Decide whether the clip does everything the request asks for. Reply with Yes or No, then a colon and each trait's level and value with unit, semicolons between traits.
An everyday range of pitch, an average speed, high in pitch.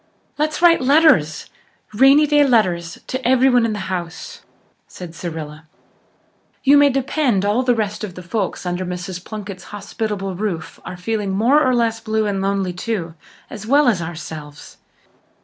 No: wide, 6.0 semitones; average, 155 wpm; high, 210 Hz